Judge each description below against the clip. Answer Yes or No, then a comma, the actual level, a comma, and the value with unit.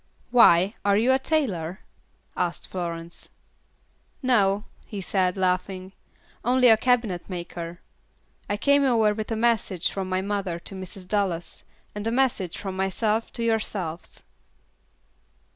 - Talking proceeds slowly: Yes, slow, 125 wpm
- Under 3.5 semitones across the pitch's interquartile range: No, average, 3.8 semitones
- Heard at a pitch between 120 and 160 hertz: No, high, 195 Hz